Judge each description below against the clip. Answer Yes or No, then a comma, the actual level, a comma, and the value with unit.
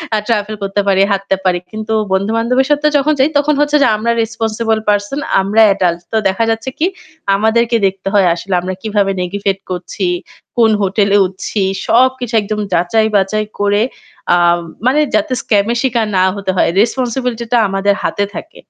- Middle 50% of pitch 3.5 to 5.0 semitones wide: No, average, 3.1 semitones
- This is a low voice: No, high, 215 Hz